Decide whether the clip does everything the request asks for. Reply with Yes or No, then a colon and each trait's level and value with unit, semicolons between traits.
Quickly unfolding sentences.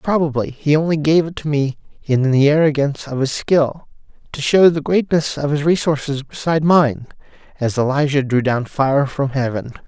No: average, 175 wpm